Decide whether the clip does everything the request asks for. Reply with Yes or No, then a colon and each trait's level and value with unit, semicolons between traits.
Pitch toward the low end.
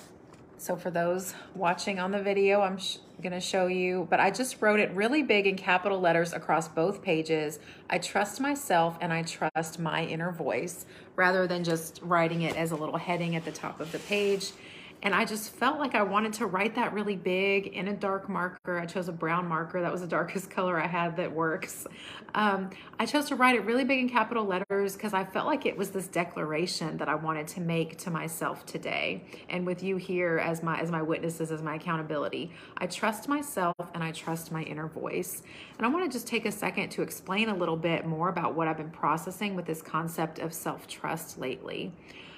No: medium, 180 Hz